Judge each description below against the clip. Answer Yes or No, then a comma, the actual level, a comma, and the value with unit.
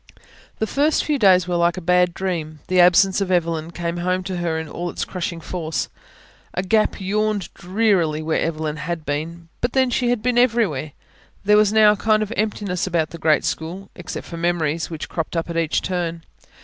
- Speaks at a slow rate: No, average, 200 wpm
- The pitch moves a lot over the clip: No, average, 3.8 semitones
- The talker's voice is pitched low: No, medium, 175 Hz